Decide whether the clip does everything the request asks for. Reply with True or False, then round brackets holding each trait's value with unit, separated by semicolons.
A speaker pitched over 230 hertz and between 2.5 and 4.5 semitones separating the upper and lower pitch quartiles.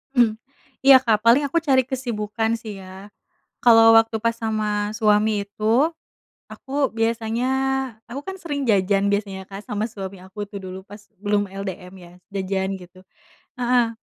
False (215 Hz; 2.8 semitones)